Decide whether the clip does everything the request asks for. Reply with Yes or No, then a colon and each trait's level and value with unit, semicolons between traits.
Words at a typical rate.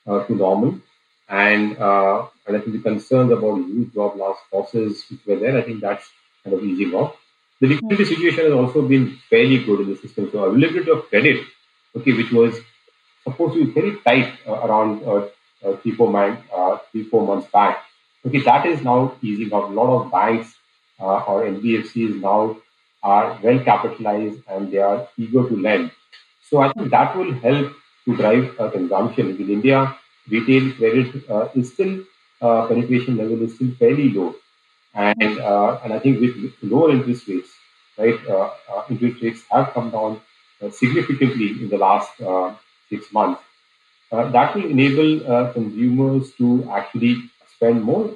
Yes: average, 175 wpm